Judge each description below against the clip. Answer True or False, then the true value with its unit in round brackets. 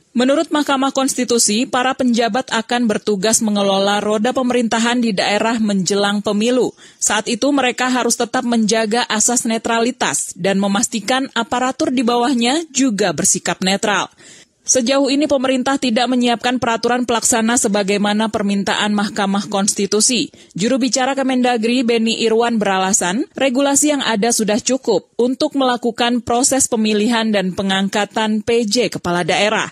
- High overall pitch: True (235 Hz)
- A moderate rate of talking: True (125 wpm)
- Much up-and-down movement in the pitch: False (3.4 semitones)